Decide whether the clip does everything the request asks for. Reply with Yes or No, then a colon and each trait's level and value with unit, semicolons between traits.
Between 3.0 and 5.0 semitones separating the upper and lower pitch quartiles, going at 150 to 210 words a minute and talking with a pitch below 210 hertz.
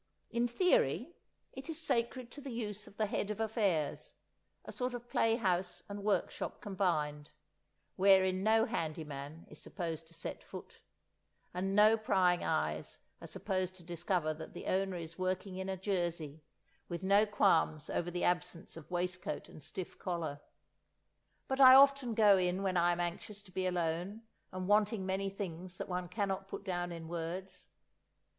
Yes: average, 3.3 semitones; average, 170 wpm; medium, 185 Hz